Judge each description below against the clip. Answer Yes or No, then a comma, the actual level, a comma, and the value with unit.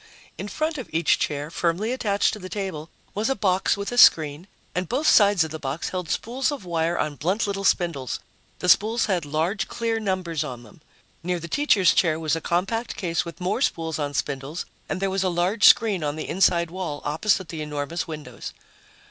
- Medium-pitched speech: Yes, medium, 180 Hz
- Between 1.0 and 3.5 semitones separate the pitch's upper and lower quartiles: No, average, 4.2 semitones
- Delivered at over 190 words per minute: Yes, fast, 205 wpm